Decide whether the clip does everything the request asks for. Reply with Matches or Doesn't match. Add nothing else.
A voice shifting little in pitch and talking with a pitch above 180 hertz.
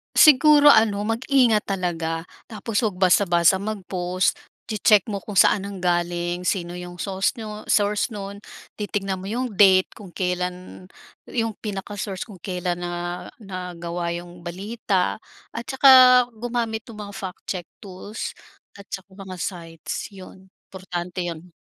Doesn't match